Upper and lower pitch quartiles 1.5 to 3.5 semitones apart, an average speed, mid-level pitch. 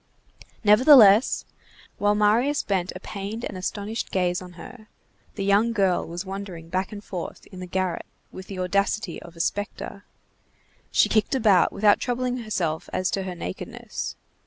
No: average, 2.7 semitones; average, 160 wpm; high, 200 Hz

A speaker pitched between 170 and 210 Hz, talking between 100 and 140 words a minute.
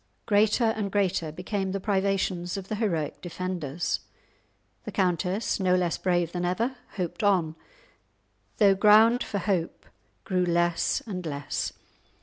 Yes: medium, 185 Hz; slow, 135 wpm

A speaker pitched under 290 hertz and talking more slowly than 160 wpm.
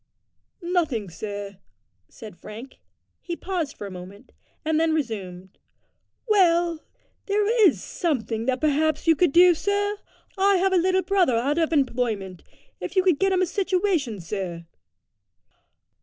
No: very high, 315 Hz; average, 140 wpm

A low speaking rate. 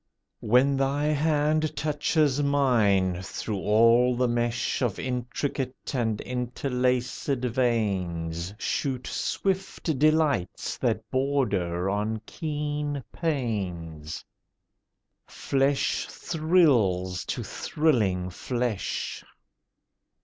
Yes: slow, 80 wpm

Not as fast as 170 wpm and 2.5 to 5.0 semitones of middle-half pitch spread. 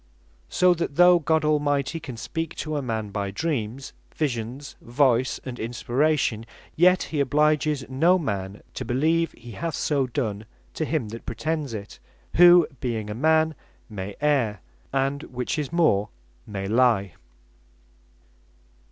No: average, 140 wpm; wide, 5.5 semitones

